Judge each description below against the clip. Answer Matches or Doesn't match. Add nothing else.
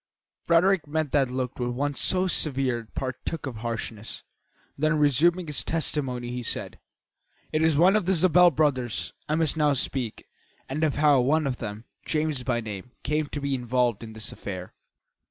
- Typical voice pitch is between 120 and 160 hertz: Matches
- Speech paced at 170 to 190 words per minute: Matches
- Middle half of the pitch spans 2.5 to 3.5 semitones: Doesn't match